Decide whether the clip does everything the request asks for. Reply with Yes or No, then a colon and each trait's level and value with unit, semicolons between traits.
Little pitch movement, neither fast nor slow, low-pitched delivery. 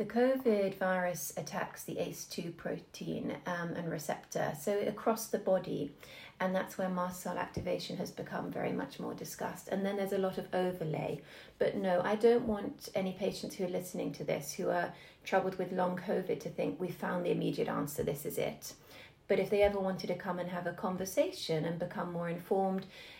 No: narrow, 1.9 semitones; average, 195 wpm; high, 190 Hz